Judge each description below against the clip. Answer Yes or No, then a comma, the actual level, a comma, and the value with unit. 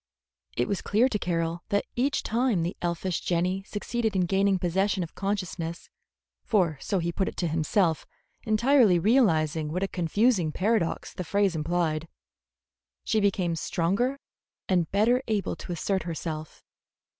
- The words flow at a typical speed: Yes, average, 145 wpm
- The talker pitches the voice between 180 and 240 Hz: Yes, medium, 185 Hz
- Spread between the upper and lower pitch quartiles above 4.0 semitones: No, average, 3.6 semitones